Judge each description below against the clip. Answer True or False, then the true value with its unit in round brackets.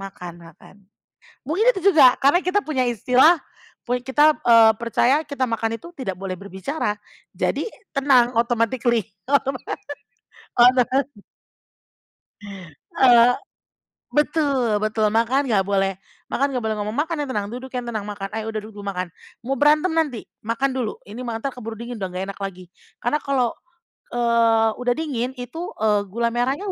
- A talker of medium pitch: False (240 Hz)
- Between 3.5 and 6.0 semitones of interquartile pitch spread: True (4.0 semitones)